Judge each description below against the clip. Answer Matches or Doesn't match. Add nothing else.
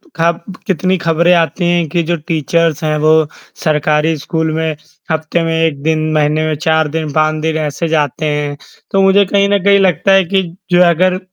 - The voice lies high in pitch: Doesn't match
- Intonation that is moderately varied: Doesn't match